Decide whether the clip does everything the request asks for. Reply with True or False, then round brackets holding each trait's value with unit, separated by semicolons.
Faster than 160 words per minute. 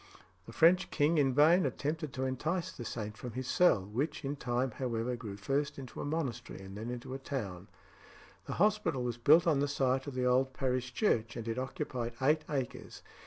True (200 wpm)